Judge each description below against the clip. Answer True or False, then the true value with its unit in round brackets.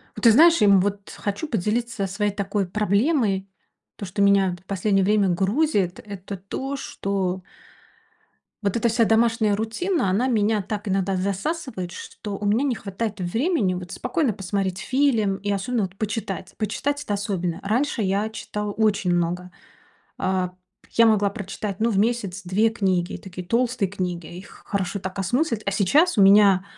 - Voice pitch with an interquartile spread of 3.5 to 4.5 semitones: False (2.9 semitones)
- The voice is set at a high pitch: True (205 Hz)